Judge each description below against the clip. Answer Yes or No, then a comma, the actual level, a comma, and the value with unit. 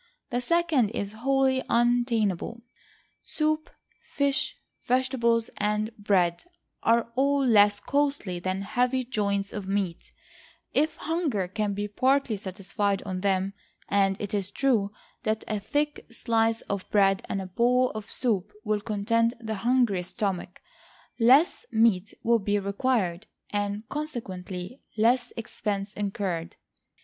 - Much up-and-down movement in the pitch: No, average, 3.9 semitones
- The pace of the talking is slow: Yes, slow, 125 wpm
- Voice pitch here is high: Yes, high, 215 Hz